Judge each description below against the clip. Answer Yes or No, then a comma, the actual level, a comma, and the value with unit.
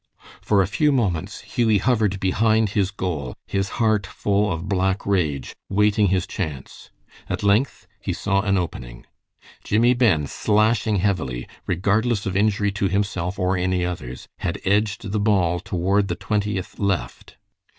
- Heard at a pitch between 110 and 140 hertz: No, low, 100 Hz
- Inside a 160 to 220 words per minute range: No, average, 150 wpm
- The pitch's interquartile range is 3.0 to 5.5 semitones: No, narrow, 2.6 semitones